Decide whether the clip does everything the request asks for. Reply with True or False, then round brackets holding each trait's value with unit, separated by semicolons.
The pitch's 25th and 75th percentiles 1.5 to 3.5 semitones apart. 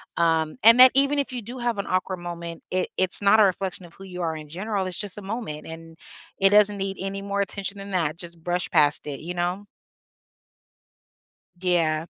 True (3.1 semitones)